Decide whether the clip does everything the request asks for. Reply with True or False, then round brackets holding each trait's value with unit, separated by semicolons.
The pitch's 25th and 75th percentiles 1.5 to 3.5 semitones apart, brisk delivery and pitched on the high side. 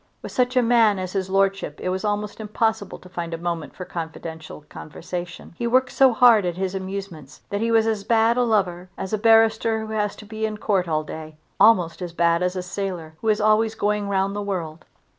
False (3.9 semitones; 220 wpm; 200 Hz)